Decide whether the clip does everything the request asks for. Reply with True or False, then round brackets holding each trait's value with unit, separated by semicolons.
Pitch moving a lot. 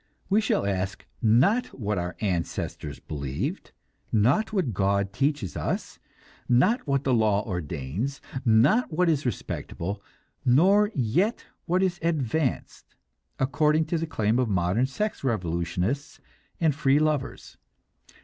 True (8.1 semitones)